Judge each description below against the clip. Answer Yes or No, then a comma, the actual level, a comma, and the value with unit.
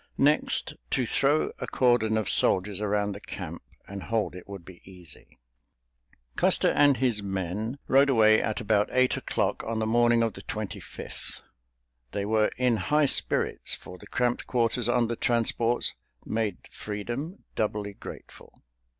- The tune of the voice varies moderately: Yes, average, 3.1 semitones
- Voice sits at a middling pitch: No, low, 110 Hz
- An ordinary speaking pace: Yes, average, 155 wpm